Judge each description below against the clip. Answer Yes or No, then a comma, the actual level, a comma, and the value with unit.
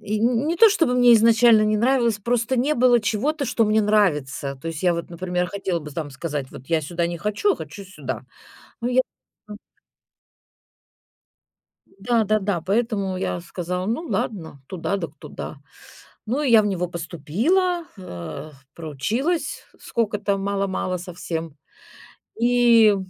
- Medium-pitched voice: No, high, 200 Hz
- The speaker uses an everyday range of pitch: No, wide, 5.8 semitones